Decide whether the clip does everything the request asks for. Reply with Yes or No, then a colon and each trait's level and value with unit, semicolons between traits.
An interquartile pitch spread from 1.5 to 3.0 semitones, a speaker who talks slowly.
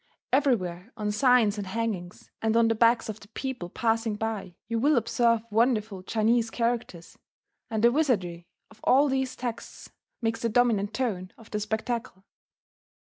No: narrow, 2.5 semitones; average, 150 wpm